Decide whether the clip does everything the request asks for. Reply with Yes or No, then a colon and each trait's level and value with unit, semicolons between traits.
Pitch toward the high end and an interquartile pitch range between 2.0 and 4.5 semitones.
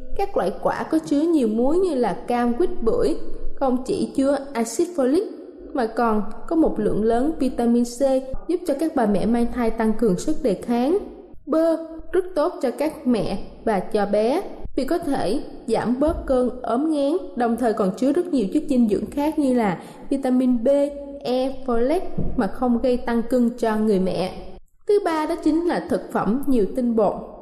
No: very high, 260 Hz; average, 5.2 semitones